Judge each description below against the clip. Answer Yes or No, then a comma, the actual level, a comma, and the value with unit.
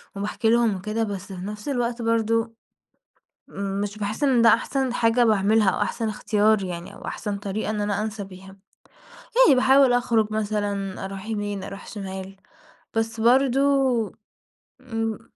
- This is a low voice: No, high, 215 Hz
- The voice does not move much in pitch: Yes, narrow, 2.3 semitones